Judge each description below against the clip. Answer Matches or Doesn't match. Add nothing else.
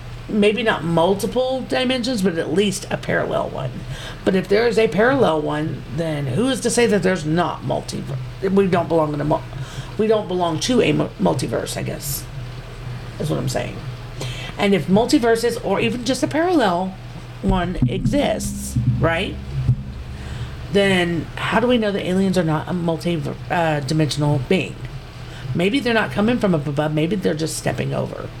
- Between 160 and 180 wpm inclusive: Matches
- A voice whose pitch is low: Doesn't match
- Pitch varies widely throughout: Matches